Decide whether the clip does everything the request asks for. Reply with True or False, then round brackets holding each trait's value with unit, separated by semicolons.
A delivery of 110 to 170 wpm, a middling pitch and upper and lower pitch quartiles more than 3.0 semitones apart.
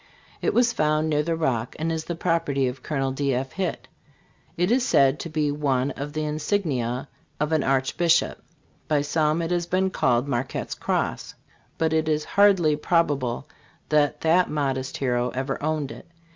False (180 wpm; 150 Hz; 3.5 semitones)